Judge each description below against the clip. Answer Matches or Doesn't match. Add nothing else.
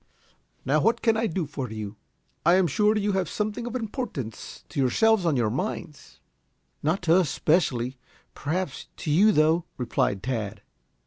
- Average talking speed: Matches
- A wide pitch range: Matches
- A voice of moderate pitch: Matches